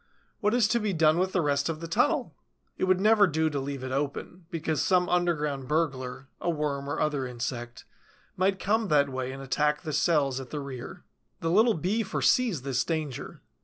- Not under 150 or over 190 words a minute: No, average, 200 wpm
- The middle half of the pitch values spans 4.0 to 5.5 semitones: Yes, average, 4.8 semitones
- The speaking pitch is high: No, medium, 155 Hz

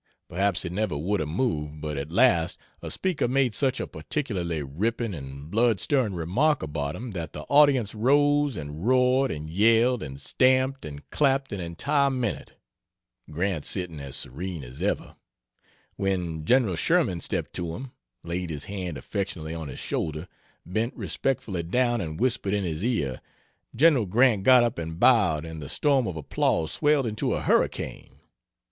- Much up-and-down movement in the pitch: Yes, wide, 8.0 semitones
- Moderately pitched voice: No, very low, 95 Hz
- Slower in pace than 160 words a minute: No, average, 165 wpm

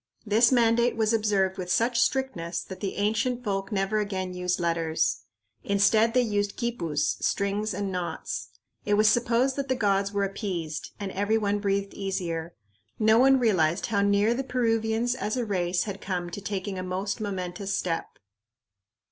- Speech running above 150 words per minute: Yes, average, 165 wpm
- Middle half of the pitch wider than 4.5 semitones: No, average, 3.2 semitones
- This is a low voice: No, high, 205 Hz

